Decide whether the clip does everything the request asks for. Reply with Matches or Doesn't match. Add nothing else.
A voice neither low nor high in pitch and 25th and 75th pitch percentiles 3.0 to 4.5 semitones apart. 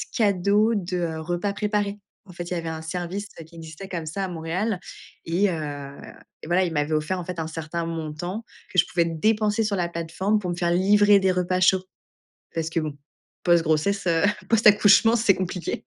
Matches